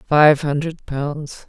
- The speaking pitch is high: No, medium, 150 Hz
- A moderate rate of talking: No, slow, 120 wpm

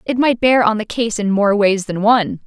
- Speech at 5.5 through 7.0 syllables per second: No, 5.2 syllables/s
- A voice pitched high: Yes, high, 215 Hz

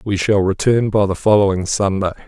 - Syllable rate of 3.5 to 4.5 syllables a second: No, 5.4 syllables/s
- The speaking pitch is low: Yes, low, 100 Hz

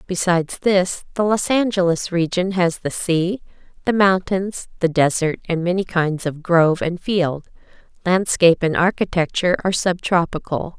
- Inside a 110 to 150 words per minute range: Yes, average, 145 wpm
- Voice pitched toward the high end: No, medium, 180 Hz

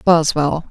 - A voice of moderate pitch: Yes, medium, 160 Hz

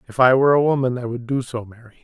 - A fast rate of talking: Yes, fast, 295 wpm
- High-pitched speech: No, low, 125 Hz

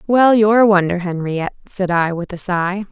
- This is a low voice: No, high, 190 Hz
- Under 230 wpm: Yes, fast, 205 wpm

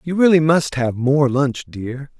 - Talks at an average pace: Yes, average, 190 wpm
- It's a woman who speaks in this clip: No, male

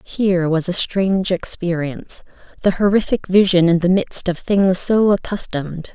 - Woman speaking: Yes, female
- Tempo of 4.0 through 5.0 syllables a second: Yes, 4.8 syllables/s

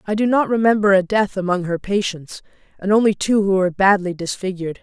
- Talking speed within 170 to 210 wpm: Yes, average, 200 wpm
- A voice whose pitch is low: No, high, 195 Hz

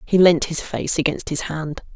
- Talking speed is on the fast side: Yes, fast, 215 wpm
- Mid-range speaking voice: Yes, medium, 160 Hz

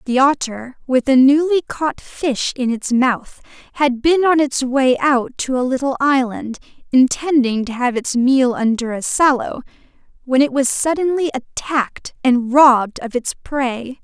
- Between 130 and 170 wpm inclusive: Yes, average, 160 wpm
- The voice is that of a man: No, female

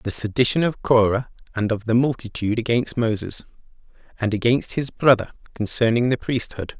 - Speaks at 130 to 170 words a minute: Yes, average, 150 wpm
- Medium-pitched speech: No, low, 115 Hz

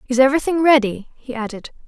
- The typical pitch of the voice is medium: No, very high, 255 Hz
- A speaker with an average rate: Yes, average, 160 wpm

